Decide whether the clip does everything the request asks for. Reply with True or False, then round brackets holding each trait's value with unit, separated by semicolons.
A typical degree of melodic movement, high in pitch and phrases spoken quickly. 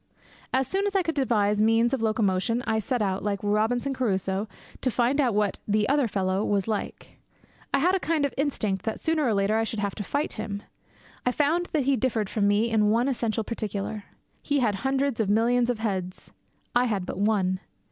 True (4.2 semitones; 225 Hz; 210 wpm)